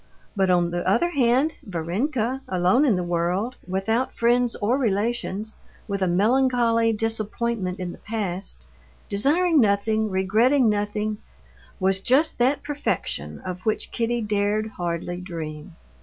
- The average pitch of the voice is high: Yes, high, 215 Hz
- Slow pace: Yes, slow, 130 wpm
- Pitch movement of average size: Yes, average, 4.3 semitones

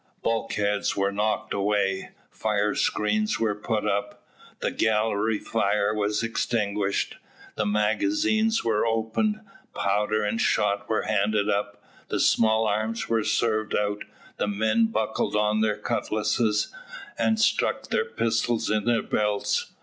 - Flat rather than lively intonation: Yes, narrow, 1.6 semitones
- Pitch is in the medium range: No, low, 105 Hz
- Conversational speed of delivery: No, slow, 125 wpm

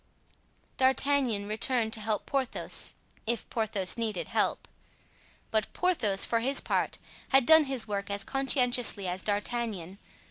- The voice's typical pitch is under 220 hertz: No, high, 225 Hz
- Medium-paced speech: No, slow, 130 wpm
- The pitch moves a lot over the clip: No, average, 4.4 semitones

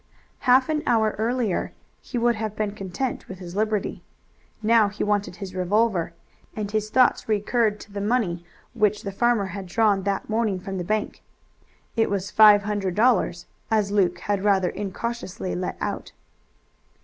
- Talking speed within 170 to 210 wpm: No, average, 160 wpm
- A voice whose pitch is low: No, high, 210 Hz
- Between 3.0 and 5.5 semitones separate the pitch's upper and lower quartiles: No, narrow, 2.5 semitones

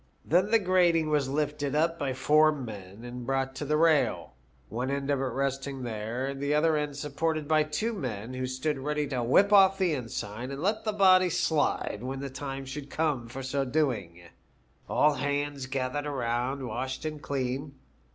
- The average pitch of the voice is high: No, medium, 140 Hz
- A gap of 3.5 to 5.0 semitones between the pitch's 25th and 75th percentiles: No, average, 3.0 semitones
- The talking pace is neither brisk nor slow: Yes, average, 180 wpm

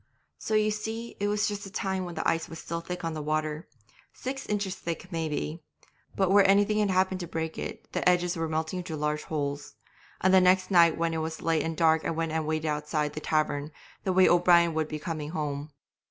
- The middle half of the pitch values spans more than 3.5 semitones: No, average, 3.2 semitones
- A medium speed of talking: No, fast, 225 wpm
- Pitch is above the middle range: No, medium, 165 Hz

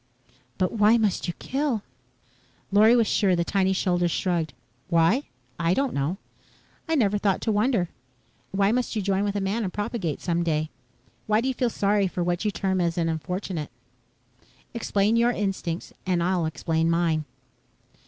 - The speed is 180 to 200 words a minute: No, average, 165 wpm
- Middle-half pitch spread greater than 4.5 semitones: No, average, 3.8 semitones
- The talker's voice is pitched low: No, high, 195 Hz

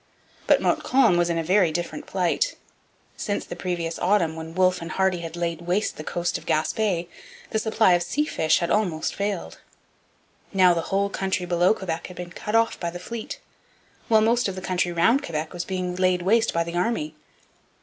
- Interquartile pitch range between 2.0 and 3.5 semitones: Yes, average, 3.0 semitones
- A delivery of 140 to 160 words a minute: No, average, 195 wpm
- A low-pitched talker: No, medium, 180 Hz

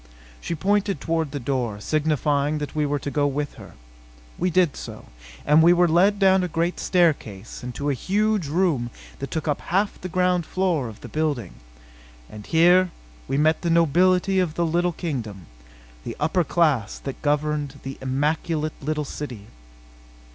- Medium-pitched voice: Yes, medium, 155 Hz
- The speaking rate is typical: Yes, average, 170 wpm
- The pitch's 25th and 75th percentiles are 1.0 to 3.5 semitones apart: No, average, 3.9 semitones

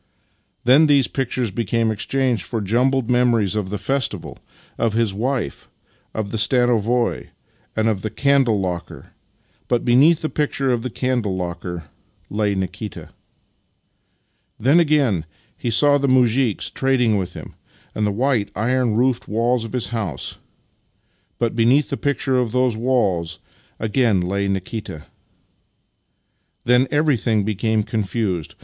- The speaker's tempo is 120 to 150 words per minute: Yes, average, 140 wpm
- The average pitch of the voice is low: Yes, low, 115 Hz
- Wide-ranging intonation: No, average, 3.8 semitones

